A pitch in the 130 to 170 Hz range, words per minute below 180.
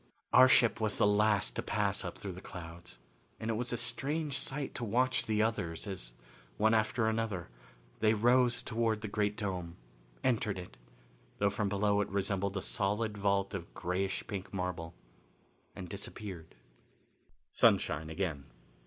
No: low, 105 Hz; average, 155 wpm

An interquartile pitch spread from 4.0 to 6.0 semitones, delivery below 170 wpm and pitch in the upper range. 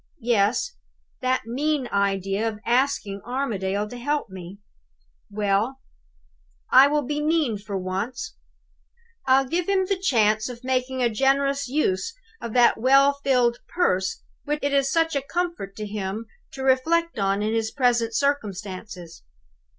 Yes: average, 5.1 semitones; average, 145 wpm; high, 245 Hz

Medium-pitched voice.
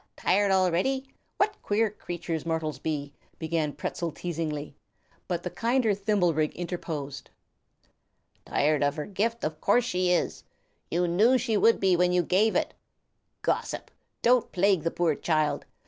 Yes: medium, 180 Hz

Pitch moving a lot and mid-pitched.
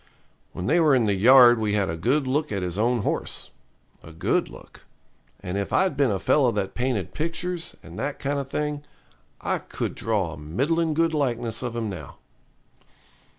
No: wide, 6.7 semitones; low, 120 Hz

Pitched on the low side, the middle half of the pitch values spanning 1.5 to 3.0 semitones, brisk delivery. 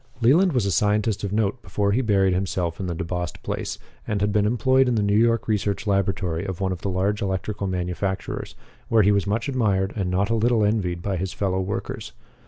Yes: low, 100 Hz; narrow, 2.5 semitones; fast, 215 wpm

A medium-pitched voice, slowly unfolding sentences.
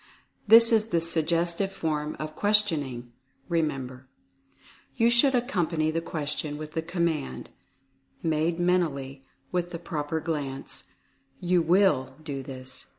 Yes: medium, 160 Hz; slow, 130 wpm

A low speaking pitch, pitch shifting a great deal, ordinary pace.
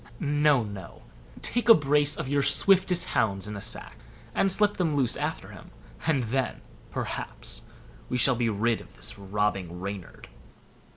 Yes: low, 125 Hz; wide, 6.4 semitones; average, 160 wpm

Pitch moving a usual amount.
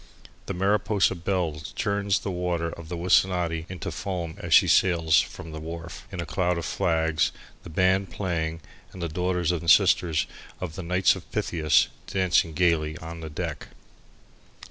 No: narrow, 2.2 semitones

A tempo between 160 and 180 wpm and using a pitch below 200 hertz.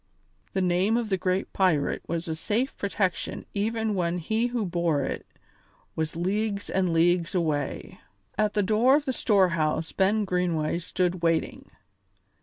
No: average, 150 wpm; medium, 185 Hz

